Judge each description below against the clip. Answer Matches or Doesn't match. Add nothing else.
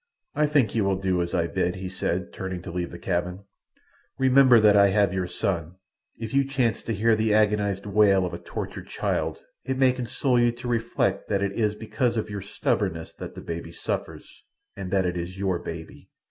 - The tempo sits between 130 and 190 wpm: Doesn't match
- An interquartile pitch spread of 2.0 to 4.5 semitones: Matches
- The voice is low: Matches